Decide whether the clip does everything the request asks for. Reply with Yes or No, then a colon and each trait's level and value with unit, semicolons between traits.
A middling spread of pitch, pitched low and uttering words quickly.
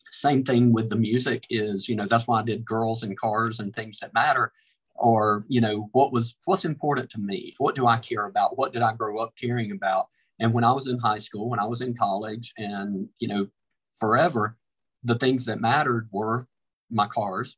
No: narrow, 2.1 semitones; low, 115 Hz; fast, 215 wpm